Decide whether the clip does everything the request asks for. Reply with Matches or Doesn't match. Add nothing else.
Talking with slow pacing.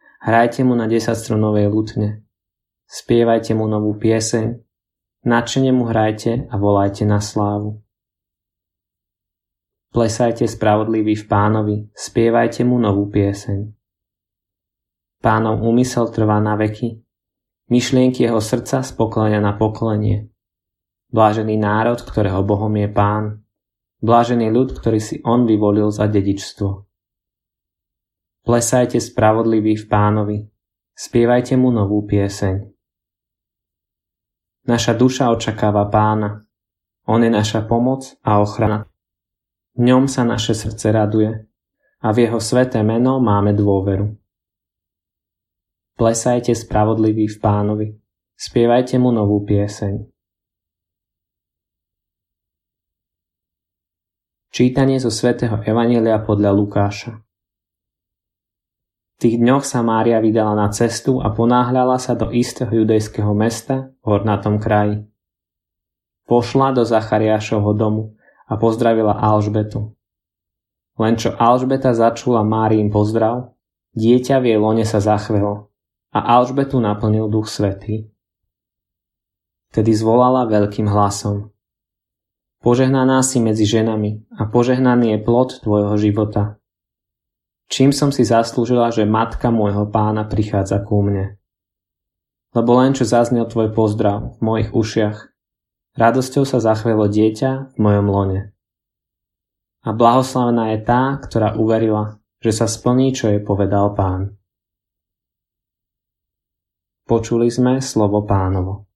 Matches